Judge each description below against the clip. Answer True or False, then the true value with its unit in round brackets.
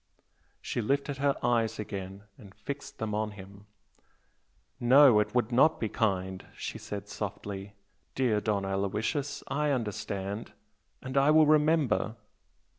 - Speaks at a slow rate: True (130 wpm)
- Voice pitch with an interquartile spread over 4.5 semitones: True (5.3 semitones)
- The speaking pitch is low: True (110 Hz)